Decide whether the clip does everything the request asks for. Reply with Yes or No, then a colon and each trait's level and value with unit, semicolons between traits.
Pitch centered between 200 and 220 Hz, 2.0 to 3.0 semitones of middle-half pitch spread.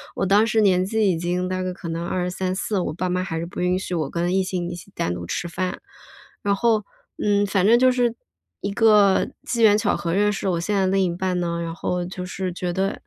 No: medium, 185 Hz; narrow, 2.5 semitones